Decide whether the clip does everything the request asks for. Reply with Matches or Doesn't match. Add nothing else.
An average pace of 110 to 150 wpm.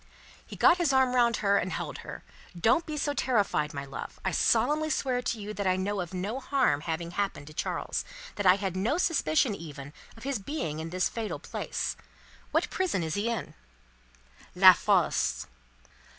Doesn't match